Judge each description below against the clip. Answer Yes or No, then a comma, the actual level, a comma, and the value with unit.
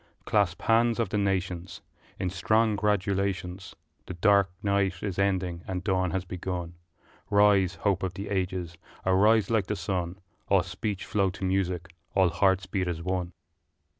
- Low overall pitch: Yes, very low, 95 Hz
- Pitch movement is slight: Yes, narrow, 1.7 semitones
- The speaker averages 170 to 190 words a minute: No, average, 155 wpm